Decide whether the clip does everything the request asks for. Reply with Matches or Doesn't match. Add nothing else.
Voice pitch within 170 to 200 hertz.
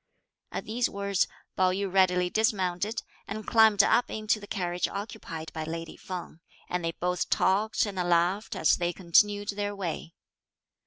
Matches